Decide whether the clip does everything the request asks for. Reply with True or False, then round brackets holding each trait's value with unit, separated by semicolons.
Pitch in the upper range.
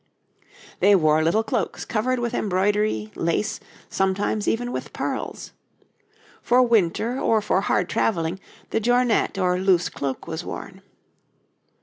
True (200 Hz)